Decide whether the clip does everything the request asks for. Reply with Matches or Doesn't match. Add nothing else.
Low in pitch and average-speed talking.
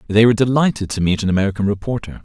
Doesn't match